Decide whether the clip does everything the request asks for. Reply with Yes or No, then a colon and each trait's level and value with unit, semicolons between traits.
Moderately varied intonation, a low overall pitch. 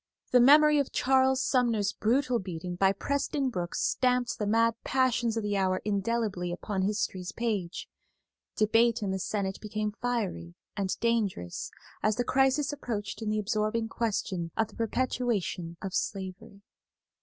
No: average, 4.0 semitones; high, 215 Hz